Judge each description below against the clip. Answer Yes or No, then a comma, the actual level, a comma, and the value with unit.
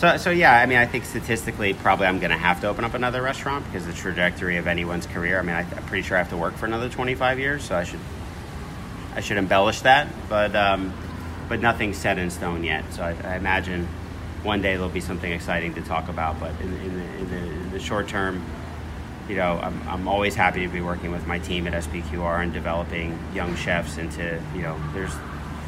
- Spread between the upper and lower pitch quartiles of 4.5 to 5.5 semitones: No, narrow, 2.6 semitones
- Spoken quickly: Yes, fast, 225 wpm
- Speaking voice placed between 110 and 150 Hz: No, very low, 90 Hz